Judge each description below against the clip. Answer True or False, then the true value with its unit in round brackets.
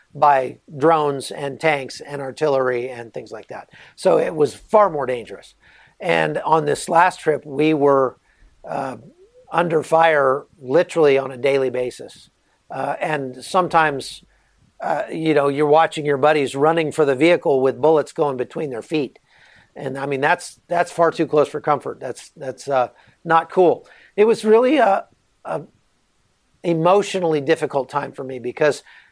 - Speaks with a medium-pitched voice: True (150 Hz)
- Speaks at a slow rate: False (160 wpm)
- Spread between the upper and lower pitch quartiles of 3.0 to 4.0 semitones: True (3.4 semitones)